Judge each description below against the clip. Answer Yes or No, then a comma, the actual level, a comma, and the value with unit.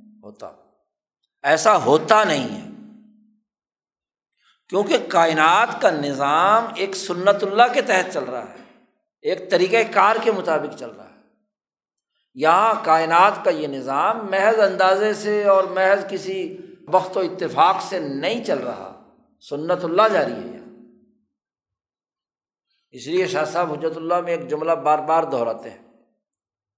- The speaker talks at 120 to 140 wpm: Yes, average, 135 wpm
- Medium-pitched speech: No, high, 195 Hz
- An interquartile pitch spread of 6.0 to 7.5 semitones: No, average, 5.2 semitones